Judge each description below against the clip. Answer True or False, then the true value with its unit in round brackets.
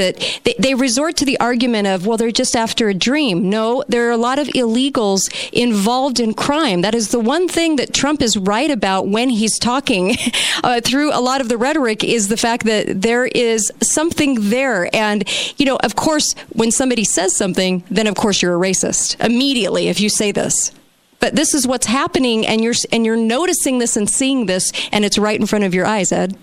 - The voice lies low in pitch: False (235 Hz)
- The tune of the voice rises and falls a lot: False (3.8 semitones)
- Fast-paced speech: True (215 wpm)